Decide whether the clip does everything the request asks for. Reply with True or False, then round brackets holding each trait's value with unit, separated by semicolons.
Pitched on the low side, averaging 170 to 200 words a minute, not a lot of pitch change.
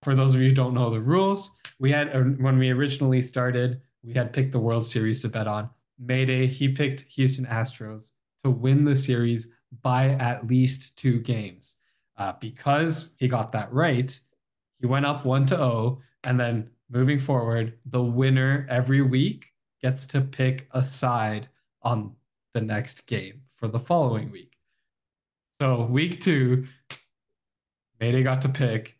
False (130 Hz; 160 wpm; 2.1 semitones)